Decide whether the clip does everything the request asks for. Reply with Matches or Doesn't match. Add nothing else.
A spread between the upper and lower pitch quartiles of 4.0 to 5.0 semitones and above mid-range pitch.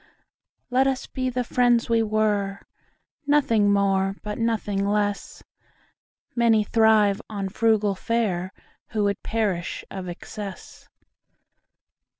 Doesn't match